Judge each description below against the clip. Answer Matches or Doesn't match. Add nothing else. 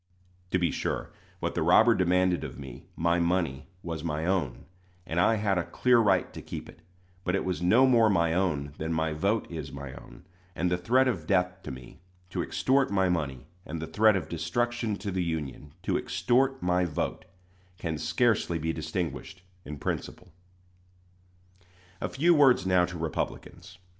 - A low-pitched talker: Matches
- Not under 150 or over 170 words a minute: Doesn't match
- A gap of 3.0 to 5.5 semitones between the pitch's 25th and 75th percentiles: Matches